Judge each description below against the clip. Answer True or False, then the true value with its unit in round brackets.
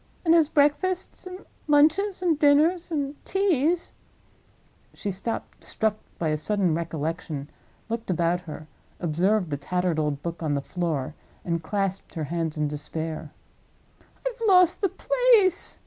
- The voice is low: False (195 Hz)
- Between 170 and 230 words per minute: False (140 wpm)